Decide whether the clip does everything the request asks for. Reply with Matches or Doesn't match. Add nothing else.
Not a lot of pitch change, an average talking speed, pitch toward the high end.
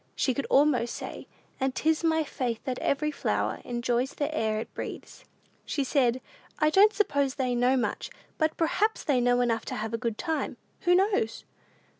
Doesn't match